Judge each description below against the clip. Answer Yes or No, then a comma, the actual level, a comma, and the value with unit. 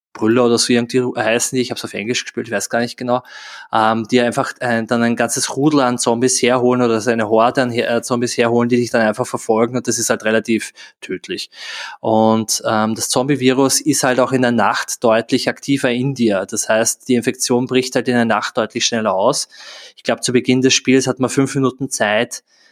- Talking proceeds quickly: Yes, fast, 220 wpm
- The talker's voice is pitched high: No, low, 120 Hz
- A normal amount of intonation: No, narrow, 2.0 semitones